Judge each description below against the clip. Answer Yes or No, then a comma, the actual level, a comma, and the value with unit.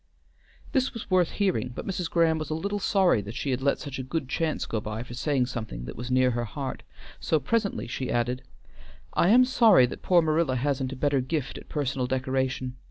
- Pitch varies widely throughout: No, average, 4.9 semitones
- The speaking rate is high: Yes, fast, 215 wpm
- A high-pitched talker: No, low, 135 Hz